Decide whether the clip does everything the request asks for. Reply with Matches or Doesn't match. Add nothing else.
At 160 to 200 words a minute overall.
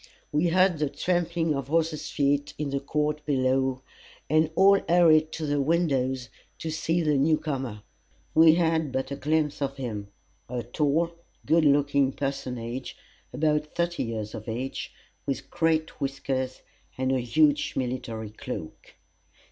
Doesn't match